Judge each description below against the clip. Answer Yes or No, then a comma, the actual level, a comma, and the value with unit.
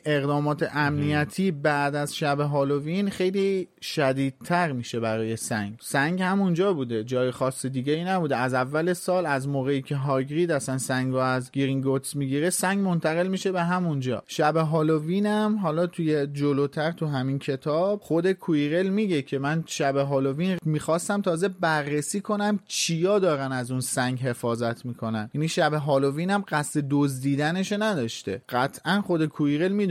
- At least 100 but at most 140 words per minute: No, average, 150 wpm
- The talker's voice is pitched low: No, medium, 150 Hz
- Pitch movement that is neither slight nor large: Yes, average, 4.7 semitones